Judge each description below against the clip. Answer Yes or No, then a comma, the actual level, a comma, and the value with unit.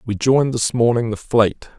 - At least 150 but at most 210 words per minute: Yes, average, 200 wpm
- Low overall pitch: Yes, low, 115 Hz